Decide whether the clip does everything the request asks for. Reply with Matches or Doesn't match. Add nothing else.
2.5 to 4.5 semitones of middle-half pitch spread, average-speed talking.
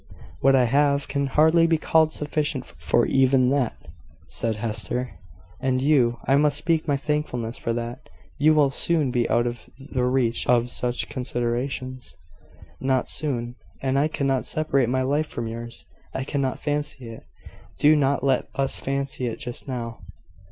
Matches